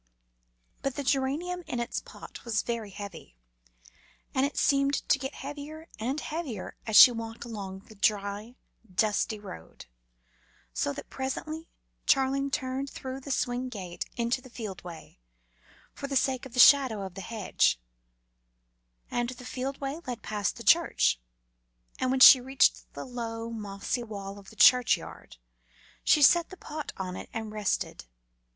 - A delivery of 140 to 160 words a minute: Yes, average, 155 wpm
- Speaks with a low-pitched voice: No, high, 245 Hz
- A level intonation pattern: No, average, 4.5 semitones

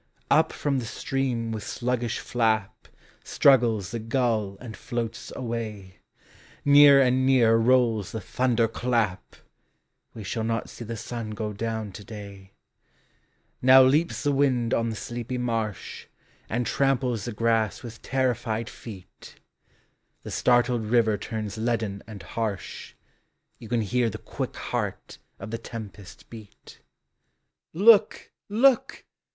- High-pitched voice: No, low, 115 Hz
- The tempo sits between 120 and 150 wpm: Yes, slow, 135 wpm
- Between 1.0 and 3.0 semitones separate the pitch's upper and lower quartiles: Yes, narrow, 2.5 semitones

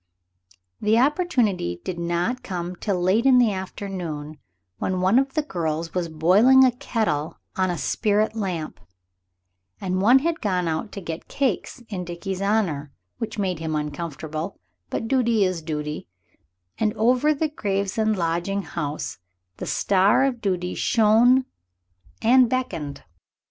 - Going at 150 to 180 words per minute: No, average, 140 wpm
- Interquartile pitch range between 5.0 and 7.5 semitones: Yes, average, 5.3 semitones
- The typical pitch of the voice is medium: No, high, 195 Hz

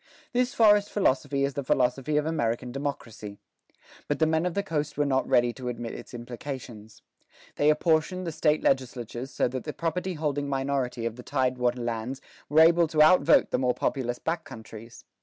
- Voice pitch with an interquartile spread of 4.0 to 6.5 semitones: Yes, average, 4.3 semitones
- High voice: No, medium, 140 Hz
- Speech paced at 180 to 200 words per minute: Yes, average, 185 wpm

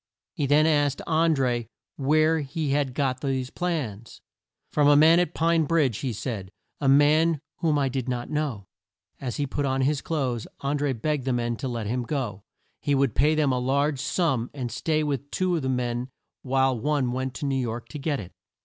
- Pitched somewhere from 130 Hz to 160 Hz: Yes, medium, 140 Hz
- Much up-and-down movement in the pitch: No, average, 3.2 semitones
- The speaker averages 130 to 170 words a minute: No, fast, 205 wpm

